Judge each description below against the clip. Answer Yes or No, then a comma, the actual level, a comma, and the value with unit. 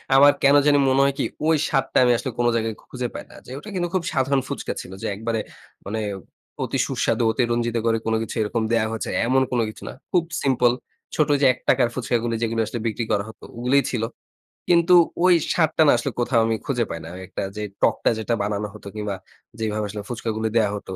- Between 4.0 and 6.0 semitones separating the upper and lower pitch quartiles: No, average, 3.4 semitones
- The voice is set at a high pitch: No, low, 120 Hz